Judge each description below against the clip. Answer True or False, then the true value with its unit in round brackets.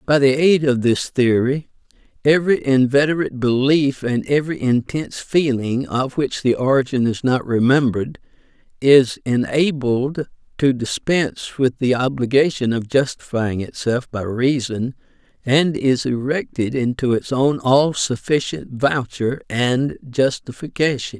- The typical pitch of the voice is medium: False (130 Hz)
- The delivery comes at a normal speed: False (120 wpm)